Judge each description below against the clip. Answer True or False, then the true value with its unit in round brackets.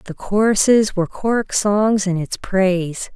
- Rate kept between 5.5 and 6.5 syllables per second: False (4.4 syllables/s)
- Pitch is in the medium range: False (200 Hz)